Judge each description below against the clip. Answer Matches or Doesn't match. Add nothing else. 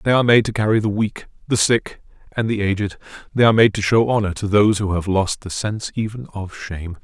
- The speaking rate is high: Matches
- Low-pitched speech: Matches